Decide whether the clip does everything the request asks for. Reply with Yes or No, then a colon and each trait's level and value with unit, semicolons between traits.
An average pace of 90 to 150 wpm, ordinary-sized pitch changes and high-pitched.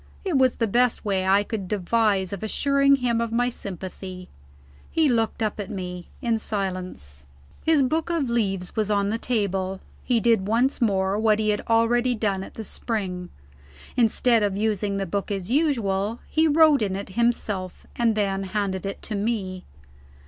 No: average, 175 wpm; average, 3.6 semitones; high, 210 Hz